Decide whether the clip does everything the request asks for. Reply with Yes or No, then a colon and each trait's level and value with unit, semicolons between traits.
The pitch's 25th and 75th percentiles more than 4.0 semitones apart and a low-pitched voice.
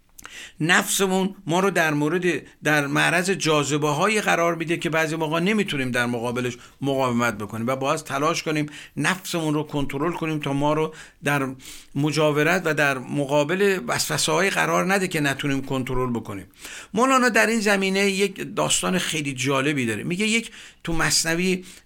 No: average, 4.7 semitones; medium, 155 Hz